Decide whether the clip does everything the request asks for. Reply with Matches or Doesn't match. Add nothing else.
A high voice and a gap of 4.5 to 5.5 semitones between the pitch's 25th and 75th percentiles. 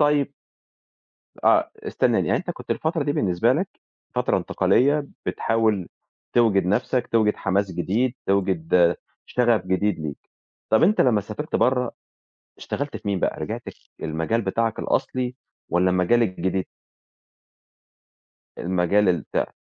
Doesn't match